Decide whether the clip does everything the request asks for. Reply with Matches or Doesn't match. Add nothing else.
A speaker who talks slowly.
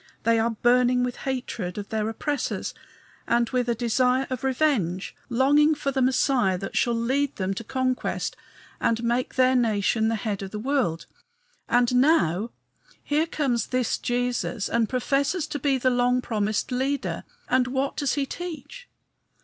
Doesn't match